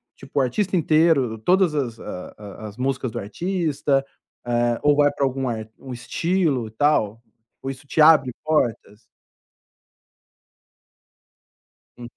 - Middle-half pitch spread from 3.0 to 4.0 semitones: No, average, 4.5 semitones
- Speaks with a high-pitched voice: No, low, 135 Hz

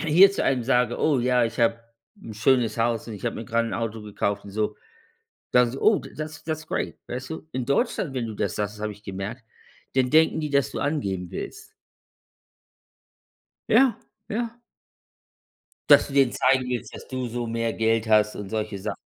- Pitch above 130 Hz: No, low, 120 Hz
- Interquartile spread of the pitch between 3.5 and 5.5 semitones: Yes, average, 4.1 semitones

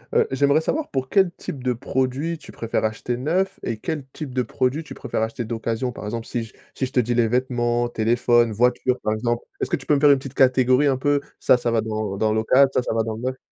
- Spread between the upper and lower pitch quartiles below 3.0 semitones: No, average, 3.3 semitones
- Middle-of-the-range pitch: No, low, 125 Hz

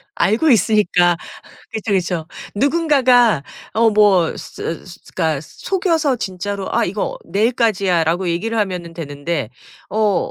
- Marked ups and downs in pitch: No, average, 4.8 semitones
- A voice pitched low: No, high, 200 Hz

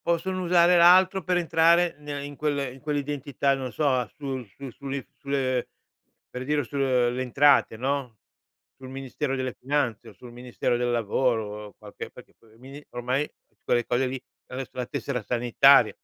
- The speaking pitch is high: No, low, 135 Hz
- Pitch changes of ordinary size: Yes, average, 3.0 semitones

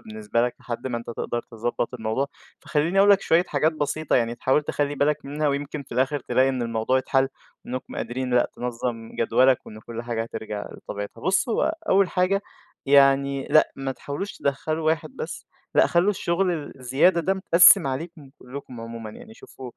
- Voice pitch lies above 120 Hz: Yes, low, 135 Hz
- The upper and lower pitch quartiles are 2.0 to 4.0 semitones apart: No, average, 4.7 semitones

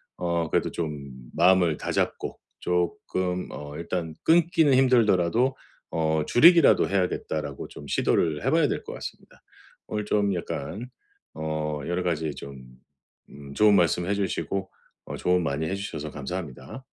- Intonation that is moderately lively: Yes, average, 4.8 semitones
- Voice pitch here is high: No, very low, 90 Hz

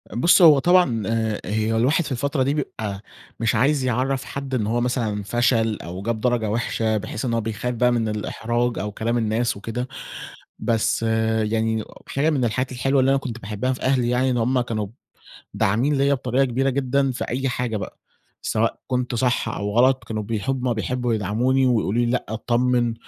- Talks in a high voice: No, low, 120 Hz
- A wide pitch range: No, average, 2.8 semitones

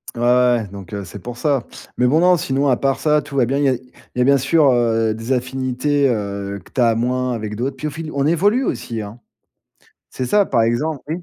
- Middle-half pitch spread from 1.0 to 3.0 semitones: No, average, 3.5 semitones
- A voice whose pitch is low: Yes, low, 125 Hz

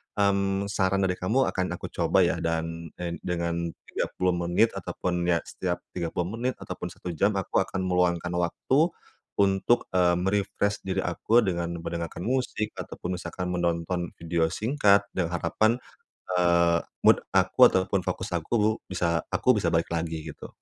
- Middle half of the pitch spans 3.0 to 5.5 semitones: No, narrow, 2.4 semitones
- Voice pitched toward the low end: Yes, very low, 90 Hz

